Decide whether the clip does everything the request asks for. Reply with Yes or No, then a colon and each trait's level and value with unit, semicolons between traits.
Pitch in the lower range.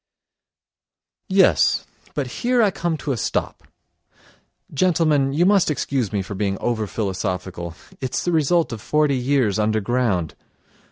Yes: low, 130 Hz